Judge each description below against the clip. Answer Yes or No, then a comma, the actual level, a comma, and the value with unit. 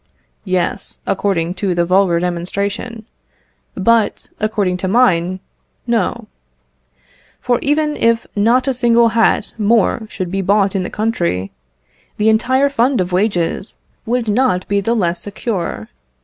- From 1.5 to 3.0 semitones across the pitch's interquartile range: No, average, 4.1 semitones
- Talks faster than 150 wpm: No, slow, 135 wpm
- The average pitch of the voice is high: Yes, high, 205 Hz